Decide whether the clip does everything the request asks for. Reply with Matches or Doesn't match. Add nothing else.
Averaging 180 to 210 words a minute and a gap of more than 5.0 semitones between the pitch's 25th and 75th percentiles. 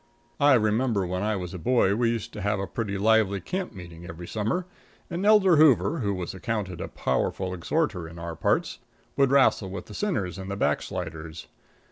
Matches